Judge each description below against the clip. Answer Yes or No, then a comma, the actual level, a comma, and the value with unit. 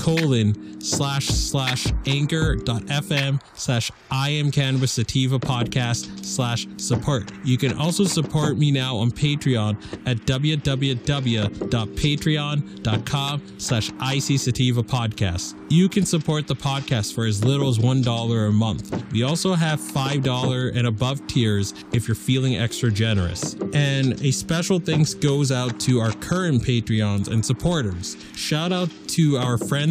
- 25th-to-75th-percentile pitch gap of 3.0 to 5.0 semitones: Yes, average, 4.2 semitones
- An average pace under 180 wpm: Yes, slow, 135 wpm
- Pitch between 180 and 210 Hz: No, low, 130 Hz